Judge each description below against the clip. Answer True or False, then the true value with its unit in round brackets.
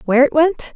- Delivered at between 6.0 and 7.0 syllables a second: True (6.6 syllables/s)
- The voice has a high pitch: True (290 Hz)